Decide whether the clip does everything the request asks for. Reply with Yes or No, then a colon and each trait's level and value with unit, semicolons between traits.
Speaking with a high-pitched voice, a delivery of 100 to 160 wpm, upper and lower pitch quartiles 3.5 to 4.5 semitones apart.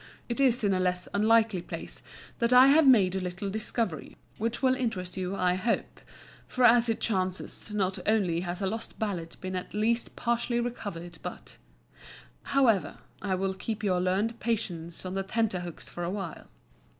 No: high, 200 Hz; average, 175 wpm; average, 4.0 semitones